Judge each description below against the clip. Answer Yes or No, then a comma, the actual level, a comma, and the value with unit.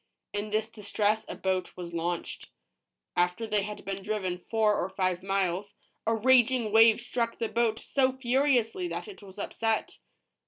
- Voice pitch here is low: No, high, 215 Hz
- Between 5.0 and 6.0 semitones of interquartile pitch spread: No, average, 3.3 semitones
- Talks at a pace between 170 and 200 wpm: No, average, 160 wpm